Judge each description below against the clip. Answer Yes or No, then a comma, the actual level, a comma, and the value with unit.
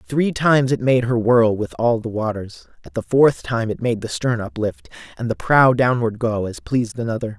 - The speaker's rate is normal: No, fast, 220 wpm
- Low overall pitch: Yes, low, 120 Hz